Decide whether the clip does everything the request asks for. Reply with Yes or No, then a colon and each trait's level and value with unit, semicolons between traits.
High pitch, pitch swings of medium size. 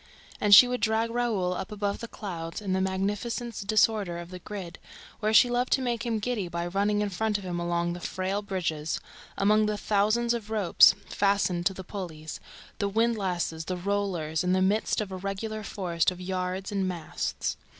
Yes: high, 195 Hz; average, 3.1 semitones